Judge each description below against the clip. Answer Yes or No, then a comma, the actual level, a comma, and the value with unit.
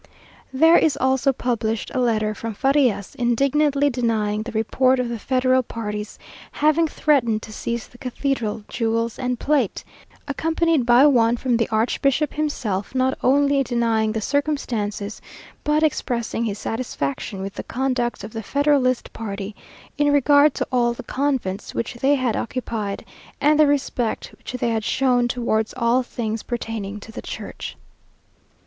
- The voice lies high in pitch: Yes, high, 245 Hz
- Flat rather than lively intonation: No, average, 3.7 semitones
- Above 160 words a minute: No, average, 150 wpm